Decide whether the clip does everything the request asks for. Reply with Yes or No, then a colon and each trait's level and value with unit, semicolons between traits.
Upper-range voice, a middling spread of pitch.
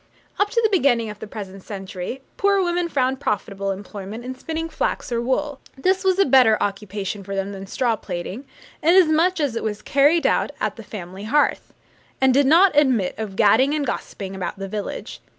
No: high, 240 Hz; wide, 6.9 semitones